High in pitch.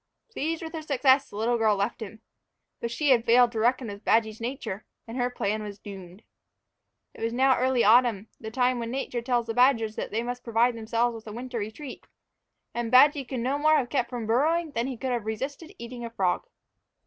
Yes: high, 240 Hz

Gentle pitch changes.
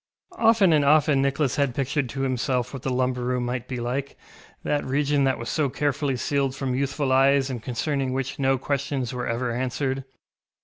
Yes: narrow, 1.9 semitones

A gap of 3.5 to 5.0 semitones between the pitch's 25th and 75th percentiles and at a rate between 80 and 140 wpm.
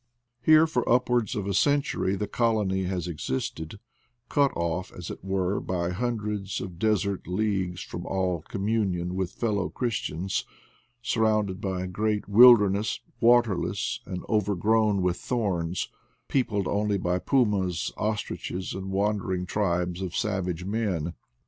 No: average, 3.0 semitones; slow, 135 wpm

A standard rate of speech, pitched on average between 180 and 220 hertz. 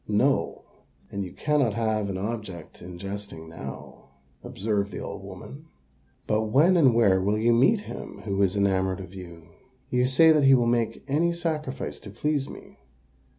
No: average, 170 wpm; low, 110 Hz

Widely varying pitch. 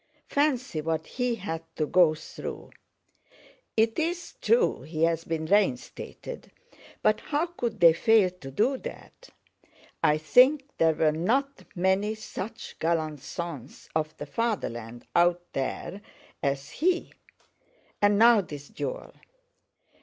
Yes: wide, 7.2 semitones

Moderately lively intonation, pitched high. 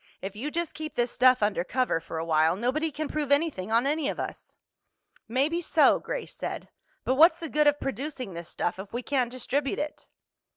No: wide, 6.2 semitones; very high, 260 Hz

